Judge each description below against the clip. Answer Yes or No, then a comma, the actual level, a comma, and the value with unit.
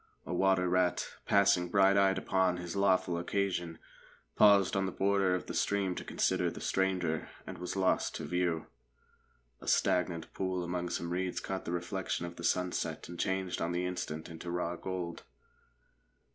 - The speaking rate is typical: Yes, average, 170 wpm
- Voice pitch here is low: Yes, very low, 90 Hz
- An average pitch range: No, narrow, 1.6 semitones